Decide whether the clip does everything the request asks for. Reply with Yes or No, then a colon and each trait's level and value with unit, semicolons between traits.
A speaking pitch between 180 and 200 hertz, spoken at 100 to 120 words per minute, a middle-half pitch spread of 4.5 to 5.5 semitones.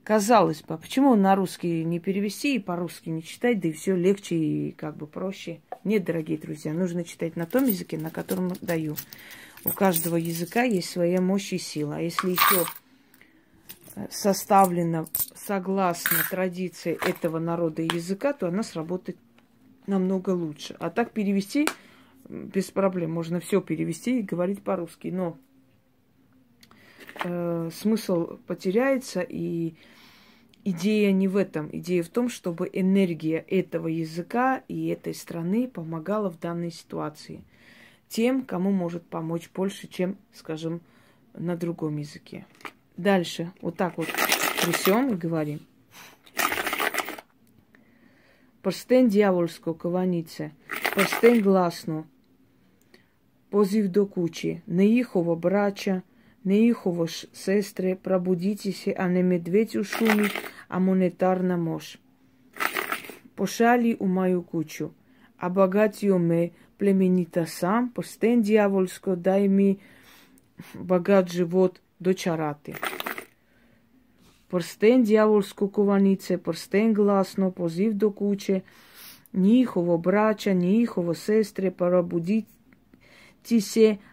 No: medium, 185 Hz; slow, 110 wpm; average, 3.3 semitones